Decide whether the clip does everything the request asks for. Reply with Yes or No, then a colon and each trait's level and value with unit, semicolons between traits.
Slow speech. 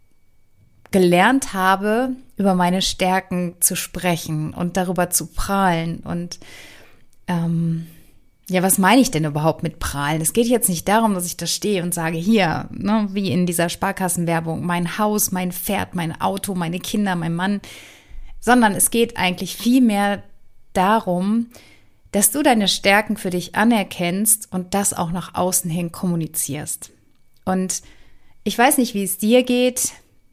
No: average, 150 wpm